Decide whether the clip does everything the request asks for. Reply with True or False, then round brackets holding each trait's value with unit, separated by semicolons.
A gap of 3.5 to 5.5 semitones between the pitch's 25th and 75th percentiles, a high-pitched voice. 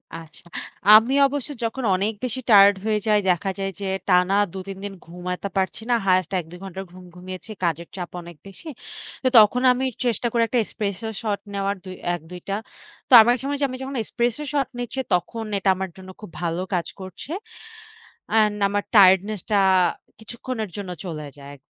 True (3.8 semitones; 200 Hz)